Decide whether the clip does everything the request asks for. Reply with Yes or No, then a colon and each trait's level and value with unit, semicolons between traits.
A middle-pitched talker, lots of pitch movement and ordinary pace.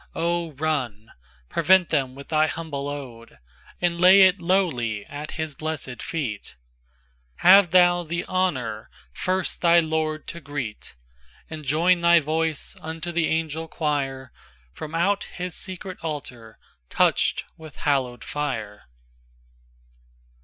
No: medium, 155 Hz; wide, 5.8 semitones; slow, 110 wpm